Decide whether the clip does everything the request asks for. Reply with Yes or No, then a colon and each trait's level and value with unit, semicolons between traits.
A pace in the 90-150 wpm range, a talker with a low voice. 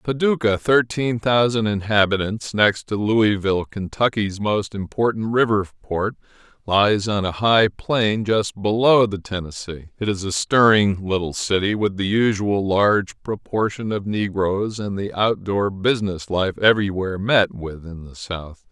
Yes: average, 145 wpm; low, 105 Hz